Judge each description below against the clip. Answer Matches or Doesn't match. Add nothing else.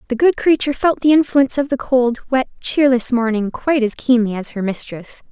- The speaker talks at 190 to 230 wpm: Matches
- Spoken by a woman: Matches